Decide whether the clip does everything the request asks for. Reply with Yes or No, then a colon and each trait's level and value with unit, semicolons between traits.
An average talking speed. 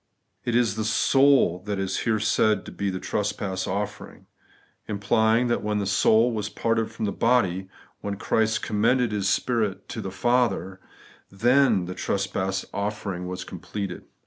Yes: average, 160 wpm